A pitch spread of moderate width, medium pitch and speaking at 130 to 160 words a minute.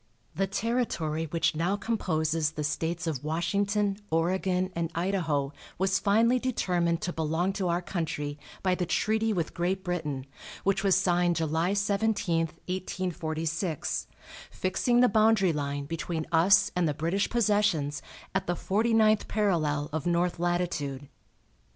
Yes: average, 3.6 semitones; medium, 175 Hz; average, 140 wpm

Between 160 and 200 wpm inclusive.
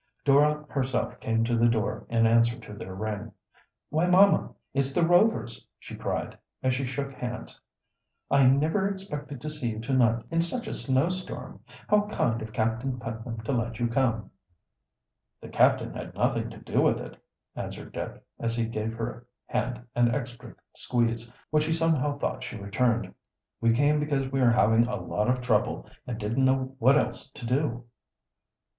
Yes: average, 175 wpm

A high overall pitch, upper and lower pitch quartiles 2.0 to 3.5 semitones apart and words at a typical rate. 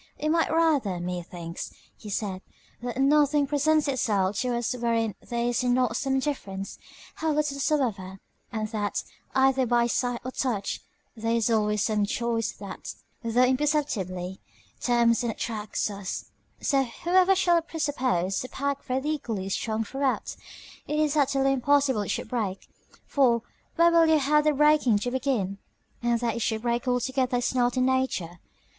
No: high, 245 Hz; average, 4.5 semitones; average, 165 wpm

